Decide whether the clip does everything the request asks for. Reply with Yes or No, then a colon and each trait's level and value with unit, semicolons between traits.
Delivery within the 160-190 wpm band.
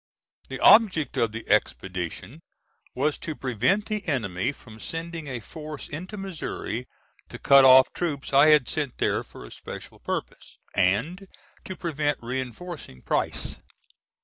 No: average, 140 wpm